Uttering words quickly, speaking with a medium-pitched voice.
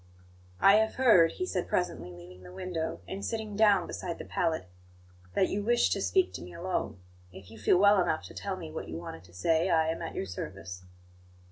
Yes: fast, 215 wpm; medium, 170 Hz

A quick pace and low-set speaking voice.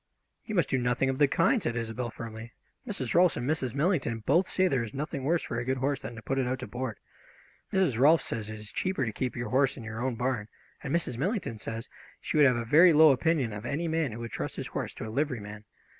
Yes: fast, 260 wpm; low, 130 Hz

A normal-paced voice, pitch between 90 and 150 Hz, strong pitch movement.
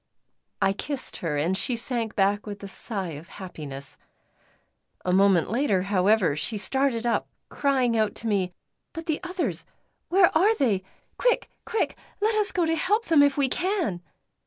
No: average, 165 wpm; high, 230 Hz; wide, 8.7 semitones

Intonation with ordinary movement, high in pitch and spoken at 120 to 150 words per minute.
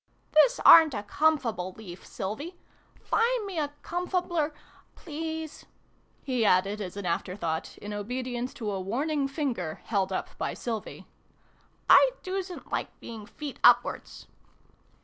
No: wide, 7.7 semitones; very high, 250 Hz; average, 145 wpm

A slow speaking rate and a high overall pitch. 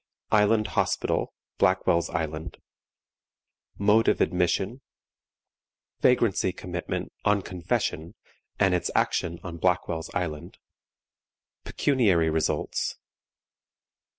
No: slow, 80 wpm; very low, 90 Hz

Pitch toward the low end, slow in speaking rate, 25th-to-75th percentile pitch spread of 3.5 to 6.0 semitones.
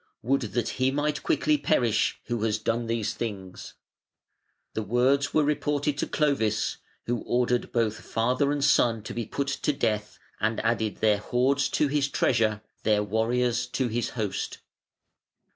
No: low, 120 Hz; average, 155 wpm; average, 3.9 semitones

